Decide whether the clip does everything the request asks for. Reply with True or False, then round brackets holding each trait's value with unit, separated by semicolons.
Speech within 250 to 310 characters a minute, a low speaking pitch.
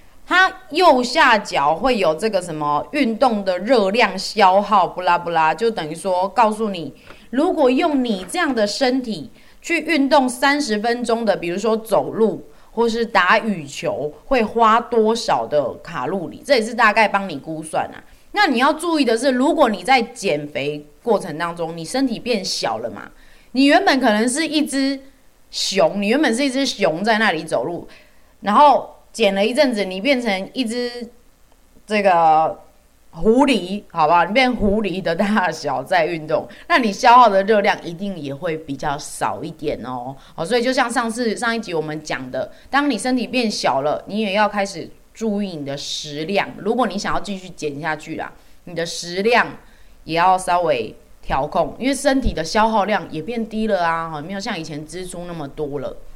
False (260 characters per minute; 215 Hz)